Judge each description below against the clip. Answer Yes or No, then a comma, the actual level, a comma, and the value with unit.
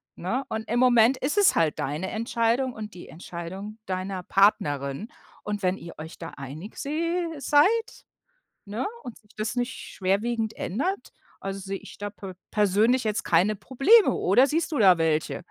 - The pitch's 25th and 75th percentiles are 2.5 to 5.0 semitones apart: No, wide, 5.4 semitones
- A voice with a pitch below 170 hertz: No, high, 215 Hz